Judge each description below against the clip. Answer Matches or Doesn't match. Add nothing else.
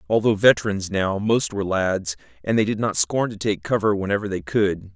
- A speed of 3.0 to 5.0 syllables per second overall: Doesn't match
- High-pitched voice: Doesn't match